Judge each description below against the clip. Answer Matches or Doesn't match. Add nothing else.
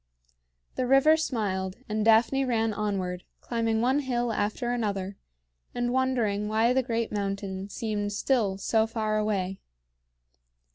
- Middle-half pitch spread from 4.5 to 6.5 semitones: Doesn't match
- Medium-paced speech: Doesn't match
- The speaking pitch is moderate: Doesn't match